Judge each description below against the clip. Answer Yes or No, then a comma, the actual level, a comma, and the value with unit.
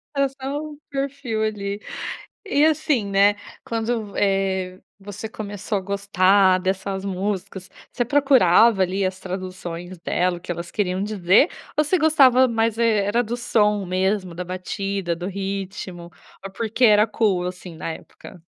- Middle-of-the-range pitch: No, high, 200 Hz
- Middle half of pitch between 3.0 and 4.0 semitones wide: Yes, average, 3.6 semitones